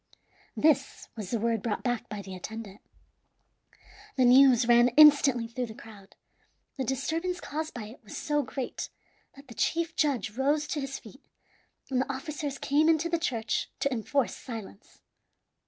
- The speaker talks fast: No, average, 160 wpm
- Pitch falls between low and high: No, very high, 260 Hz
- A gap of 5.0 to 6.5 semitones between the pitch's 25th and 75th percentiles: No, average, 4.5 semitones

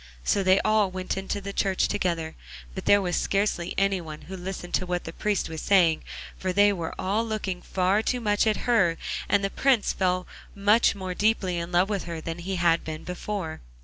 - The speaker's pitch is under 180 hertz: No, high, 190 Hz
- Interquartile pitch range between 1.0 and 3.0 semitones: Yes, narrow, 2.5 semitones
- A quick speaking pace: Yes, fast, 210 wpm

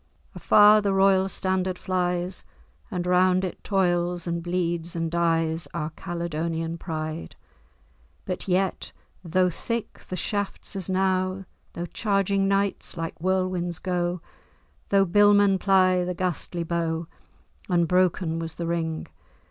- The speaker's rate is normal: No, slow, 125 wpm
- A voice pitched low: No, medium, 180 Hz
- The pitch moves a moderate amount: No, narrow, 1.9 semitones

